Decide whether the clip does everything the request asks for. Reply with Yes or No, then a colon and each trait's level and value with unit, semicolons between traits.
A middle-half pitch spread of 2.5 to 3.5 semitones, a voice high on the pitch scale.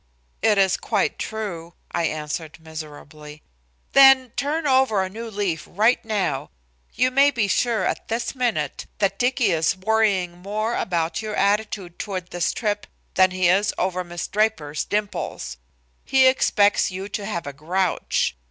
No: average, 4.3 semitones; high, 200 Hz